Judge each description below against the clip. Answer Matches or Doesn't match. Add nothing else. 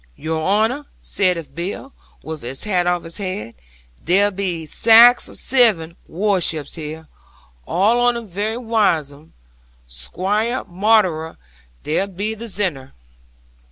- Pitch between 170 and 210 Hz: Matches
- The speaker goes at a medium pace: Doesn't match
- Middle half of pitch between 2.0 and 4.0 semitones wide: Doesn't match